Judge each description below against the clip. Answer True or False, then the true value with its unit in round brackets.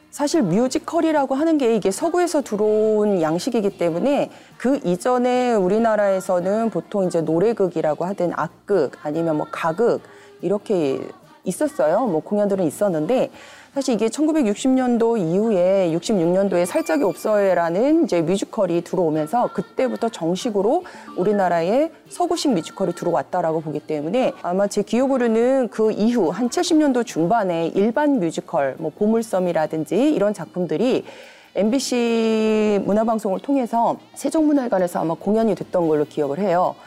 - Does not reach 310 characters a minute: False (335 characters per minute)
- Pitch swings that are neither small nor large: False (6.9 semitones)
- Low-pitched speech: False (215 Hz)